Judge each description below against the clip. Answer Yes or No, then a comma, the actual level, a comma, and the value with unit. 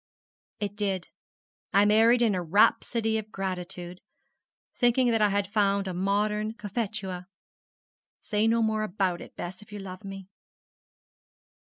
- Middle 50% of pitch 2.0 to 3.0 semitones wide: Yes, narrow, 2.4 semitones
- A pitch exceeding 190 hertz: Yes, high, 205 Hz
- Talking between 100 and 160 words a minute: Yes, average, 140 wpm